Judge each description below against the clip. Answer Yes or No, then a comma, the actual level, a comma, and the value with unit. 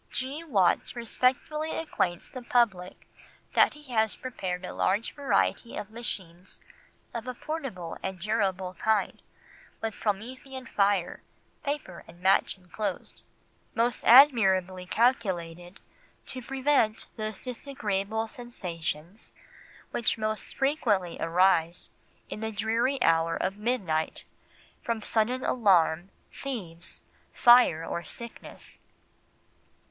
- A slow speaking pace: Yes, slow, 105 wpm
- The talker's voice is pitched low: No, high, 215 Hz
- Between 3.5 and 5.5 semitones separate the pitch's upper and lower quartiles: Yes, average, 5.1 semitones